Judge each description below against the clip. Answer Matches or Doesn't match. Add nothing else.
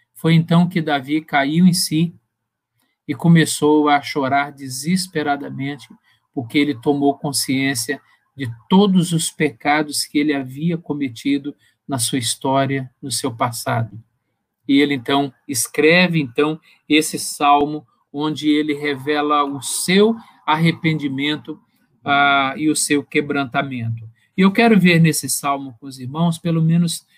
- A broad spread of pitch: Doesn't match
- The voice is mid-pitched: Matches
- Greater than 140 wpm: Doesn't match